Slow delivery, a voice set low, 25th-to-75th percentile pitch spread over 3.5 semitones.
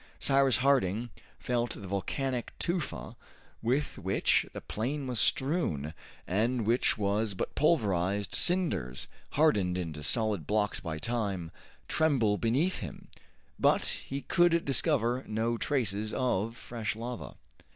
Yes: slow, 120 wpm; low, 115 Hz; average, 5.3 semitones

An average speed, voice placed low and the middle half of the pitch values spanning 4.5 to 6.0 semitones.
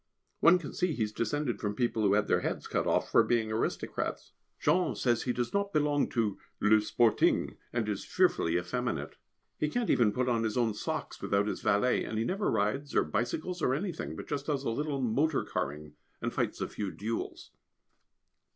Yes: average, 195 wpm; low, 120 Hz; wide, 5.5 semitones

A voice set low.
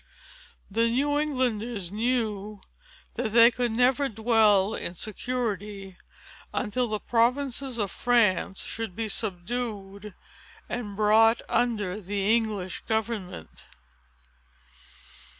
No: high, 220 Hz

